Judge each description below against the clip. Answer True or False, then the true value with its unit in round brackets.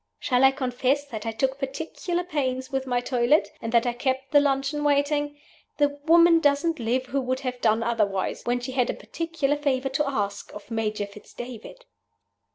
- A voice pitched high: True (265 Hz)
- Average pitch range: True (3.2 semitones)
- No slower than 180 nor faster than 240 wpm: True (185 wpm)